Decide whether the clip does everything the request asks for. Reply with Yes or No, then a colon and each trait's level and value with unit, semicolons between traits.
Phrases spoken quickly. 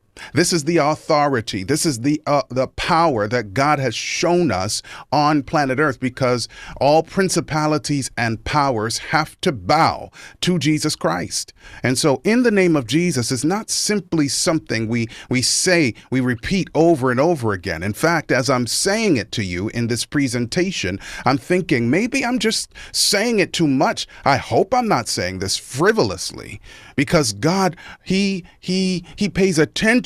No: average, 165 wpm